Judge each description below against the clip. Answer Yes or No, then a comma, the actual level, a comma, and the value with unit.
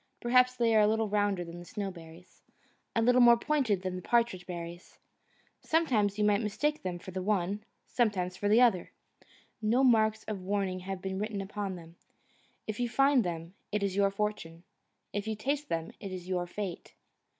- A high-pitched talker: Yes, high, 205 Hz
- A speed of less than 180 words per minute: No, average, 185 wpm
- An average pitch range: Yes, average, 3.5 semitones